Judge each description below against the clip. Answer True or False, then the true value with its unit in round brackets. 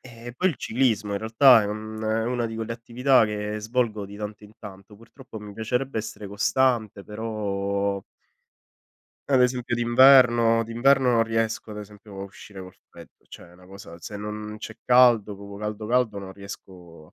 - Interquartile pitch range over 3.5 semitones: False (2.7 semitones)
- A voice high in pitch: False (110 Hz)